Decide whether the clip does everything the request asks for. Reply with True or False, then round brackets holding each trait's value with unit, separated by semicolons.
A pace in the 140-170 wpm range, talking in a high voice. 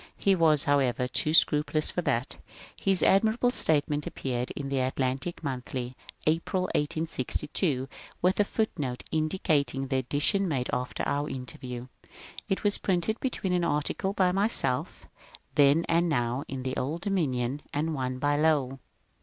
False (155 wpm; 150 Hz)